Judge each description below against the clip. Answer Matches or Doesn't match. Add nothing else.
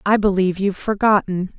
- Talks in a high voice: Matches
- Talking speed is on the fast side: Doesn't match